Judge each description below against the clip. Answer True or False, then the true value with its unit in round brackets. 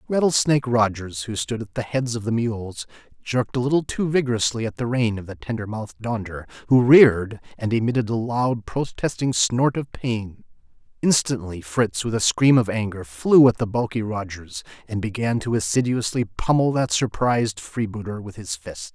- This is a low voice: True (115 Hz)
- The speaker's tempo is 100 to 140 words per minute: False (175 wpm)